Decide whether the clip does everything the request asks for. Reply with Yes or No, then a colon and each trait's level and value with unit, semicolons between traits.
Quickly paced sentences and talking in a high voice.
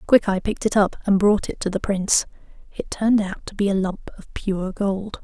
Yes: fast, 230 wpm; high, 200 Hz